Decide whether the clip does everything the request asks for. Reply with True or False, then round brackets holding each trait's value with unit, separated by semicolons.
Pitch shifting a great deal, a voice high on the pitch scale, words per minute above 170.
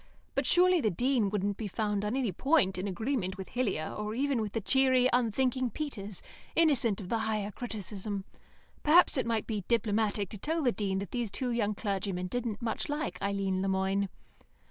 False (4.1 semitones; 215 Hz; 190 wpm)